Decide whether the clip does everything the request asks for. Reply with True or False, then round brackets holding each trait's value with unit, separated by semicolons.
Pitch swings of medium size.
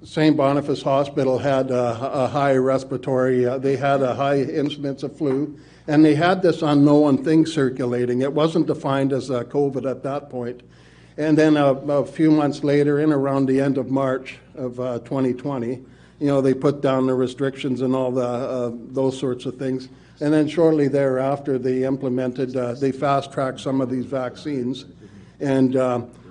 False (1.9 semitones)